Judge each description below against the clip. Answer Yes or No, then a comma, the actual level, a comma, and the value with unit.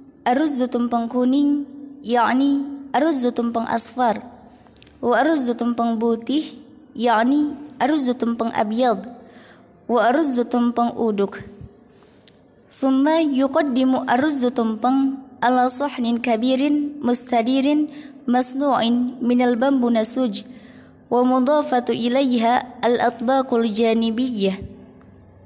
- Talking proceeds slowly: Yes, slow, 80 wpm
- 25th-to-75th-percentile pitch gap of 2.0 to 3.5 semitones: Yes, narrow, 2.6 semitones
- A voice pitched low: No, high, 245 Hz